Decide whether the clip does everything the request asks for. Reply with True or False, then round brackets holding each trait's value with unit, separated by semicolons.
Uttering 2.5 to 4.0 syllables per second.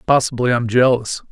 False (6.3 syllables/s)